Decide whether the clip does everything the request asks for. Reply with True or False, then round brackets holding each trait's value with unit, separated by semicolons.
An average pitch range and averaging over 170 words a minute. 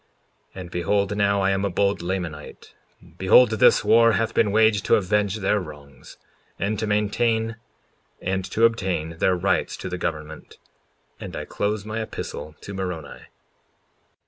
False (3.2 semitones; 155 wpm)